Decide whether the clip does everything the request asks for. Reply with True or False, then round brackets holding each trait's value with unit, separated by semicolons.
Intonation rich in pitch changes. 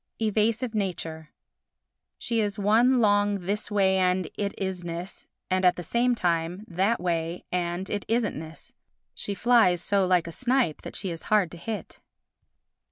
False (3.4 semitones)